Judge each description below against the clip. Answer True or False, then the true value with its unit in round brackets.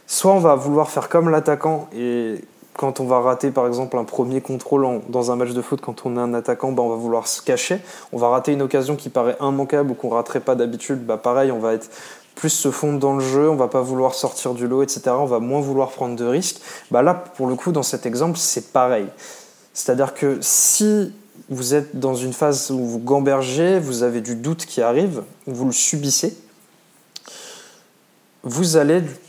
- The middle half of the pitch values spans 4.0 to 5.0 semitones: False (3.3 semitones)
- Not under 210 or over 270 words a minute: True (215 wpm)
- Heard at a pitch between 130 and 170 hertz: True (135 Hz)